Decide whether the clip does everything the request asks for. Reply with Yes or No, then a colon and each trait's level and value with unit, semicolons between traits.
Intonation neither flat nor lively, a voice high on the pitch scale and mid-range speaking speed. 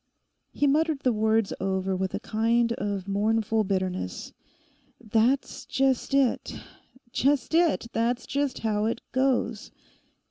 No: average, 4.3 semitones; high, 225 Hz; slow, 115 wpm